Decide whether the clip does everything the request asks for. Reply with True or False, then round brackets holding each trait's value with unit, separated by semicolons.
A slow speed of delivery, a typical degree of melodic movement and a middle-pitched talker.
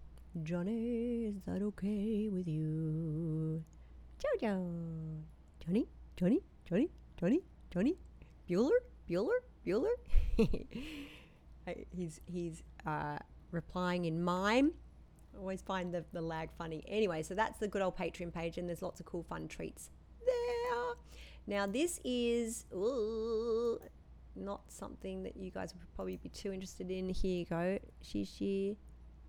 False (130 wpm; 5.7 semitones; 180 Hz)